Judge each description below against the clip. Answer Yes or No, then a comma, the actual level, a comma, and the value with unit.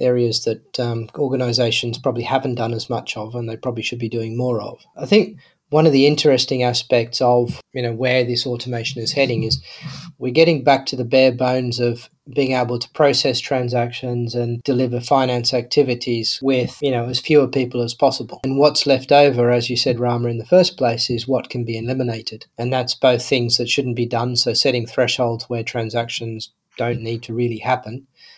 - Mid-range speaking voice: No, low, 125 Hz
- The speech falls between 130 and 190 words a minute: No, average, 200 wpm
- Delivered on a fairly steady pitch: Yes, narrow, 2.0 semitones